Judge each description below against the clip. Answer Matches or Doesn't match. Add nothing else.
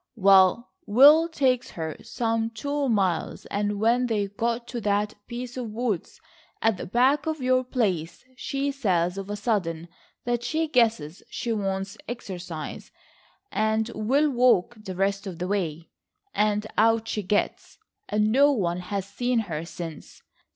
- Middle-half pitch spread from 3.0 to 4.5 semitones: Matches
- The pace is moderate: Matches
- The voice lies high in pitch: Matches